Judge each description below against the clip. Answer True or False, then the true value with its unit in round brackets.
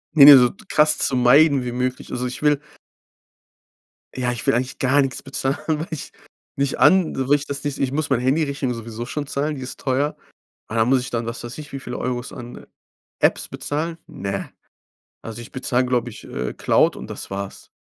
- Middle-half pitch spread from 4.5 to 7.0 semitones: False (2.9 semitones)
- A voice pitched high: False (130 Hz)